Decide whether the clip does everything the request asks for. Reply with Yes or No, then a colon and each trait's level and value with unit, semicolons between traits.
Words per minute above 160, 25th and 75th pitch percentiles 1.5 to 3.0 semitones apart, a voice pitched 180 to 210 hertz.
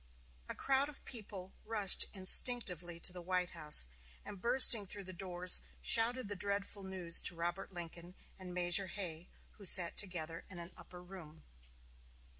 No: average, 155 wpm; narrow, 2.6 semitones; medium, 185 Hz